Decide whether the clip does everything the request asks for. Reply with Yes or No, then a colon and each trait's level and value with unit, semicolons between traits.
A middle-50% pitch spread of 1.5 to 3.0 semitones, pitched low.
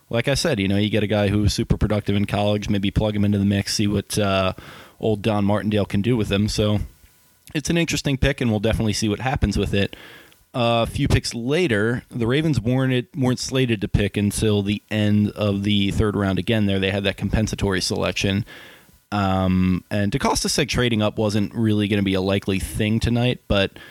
Yes: narrow, 2.6 semitones; low, 105 Hz